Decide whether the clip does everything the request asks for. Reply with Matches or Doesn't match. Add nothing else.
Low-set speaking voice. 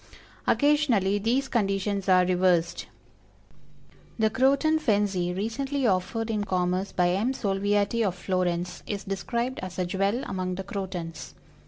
Doesn't match